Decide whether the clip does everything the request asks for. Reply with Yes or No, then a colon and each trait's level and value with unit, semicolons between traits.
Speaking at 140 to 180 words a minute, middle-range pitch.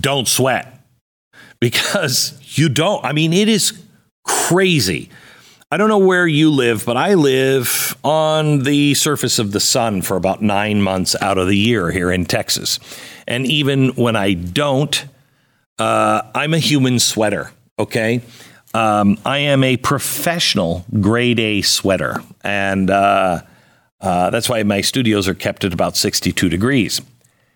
No: average, 150 wpm; low, 125 Hz